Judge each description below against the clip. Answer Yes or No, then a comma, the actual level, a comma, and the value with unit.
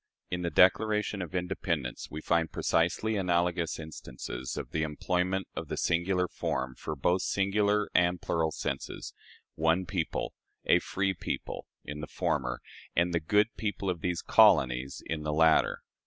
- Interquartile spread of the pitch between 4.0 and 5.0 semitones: No, average, 3.3 semitones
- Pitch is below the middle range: Yes, very low, 85 Hz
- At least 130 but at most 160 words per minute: Yes, average, 155 wpm